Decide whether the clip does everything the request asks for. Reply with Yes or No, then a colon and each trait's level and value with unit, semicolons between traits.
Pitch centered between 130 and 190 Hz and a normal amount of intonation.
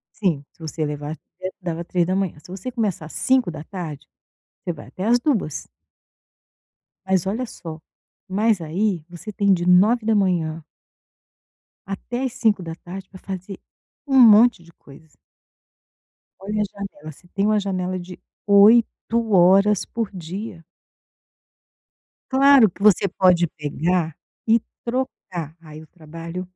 Yes: medium, 185 Hz; average, 4.2 semitones